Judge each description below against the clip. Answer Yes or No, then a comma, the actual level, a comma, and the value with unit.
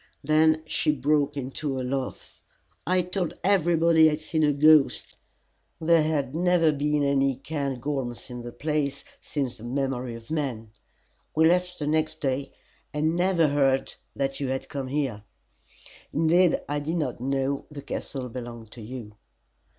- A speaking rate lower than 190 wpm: Yes, average, 155 wpm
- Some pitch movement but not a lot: Yes, average, 3.0 semitones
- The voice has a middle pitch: Yes, medium, 145 Hz